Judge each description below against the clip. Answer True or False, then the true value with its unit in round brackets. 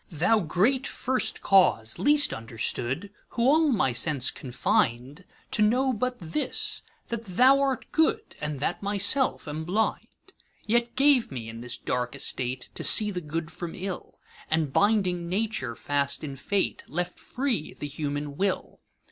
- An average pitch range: False (8.7 semitones)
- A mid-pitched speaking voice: True (180 Hz)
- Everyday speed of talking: False (130 wpm)